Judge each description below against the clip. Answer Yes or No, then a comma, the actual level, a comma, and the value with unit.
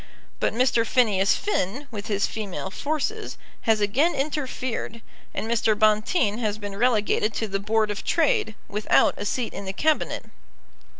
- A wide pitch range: No, average, 3.6 semitones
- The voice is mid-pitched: No, high, 220 Hz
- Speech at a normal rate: Yes, average, 155 wpm